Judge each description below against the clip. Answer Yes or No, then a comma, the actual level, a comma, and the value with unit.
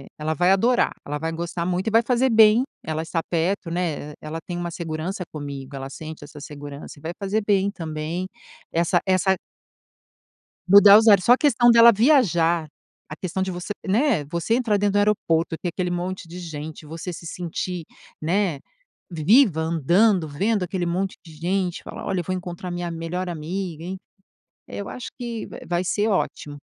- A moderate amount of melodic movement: Yes, average, 3.7 semitones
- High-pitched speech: No, medium, 175 Hz